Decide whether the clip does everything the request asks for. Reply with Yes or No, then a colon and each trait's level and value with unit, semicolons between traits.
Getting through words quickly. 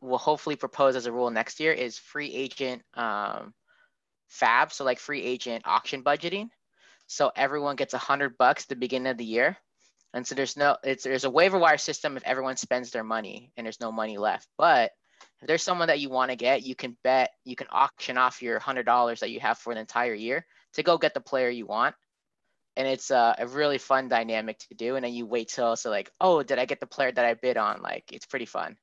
Yes: fast, 235 wpm